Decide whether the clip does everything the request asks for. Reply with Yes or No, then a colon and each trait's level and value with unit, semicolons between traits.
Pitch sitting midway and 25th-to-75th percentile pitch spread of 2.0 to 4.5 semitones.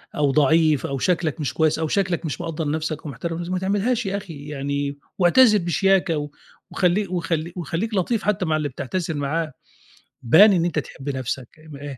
Yes: medium, 165 Hz; average, 4.0 semitones